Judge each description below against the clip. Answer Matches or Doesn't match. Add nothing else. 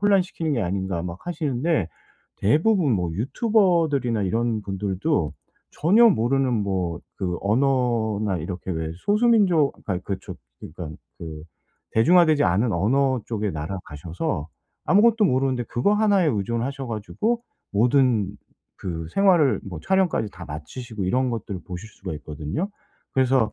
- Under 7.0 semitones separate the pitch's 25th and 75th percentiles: Doesn't match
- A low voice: Matches